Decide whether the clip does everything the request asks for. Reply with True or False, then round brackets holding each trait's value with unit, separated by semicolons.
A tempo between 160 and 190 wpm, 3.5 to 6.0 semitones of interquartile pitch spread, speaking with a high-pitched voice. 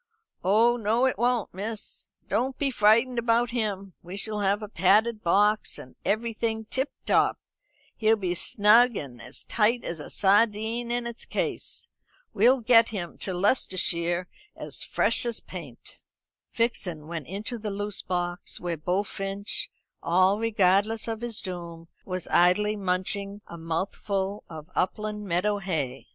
False (145 wpm; 3.8 semitones; 205 Hz)